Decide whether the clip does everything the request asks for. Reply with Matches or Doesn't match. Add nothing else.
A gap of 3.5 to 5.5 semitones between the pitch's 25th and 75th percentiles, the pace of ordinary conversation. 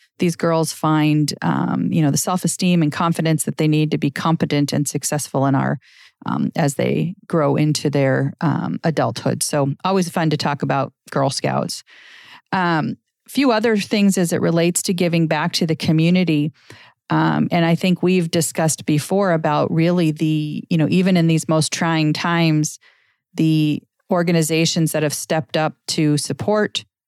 Doesn't match